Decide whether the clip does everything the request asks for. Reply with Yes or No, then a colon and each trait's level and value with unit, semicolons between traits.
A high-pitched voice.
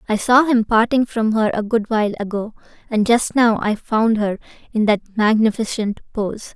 Yes: high, 220 Hz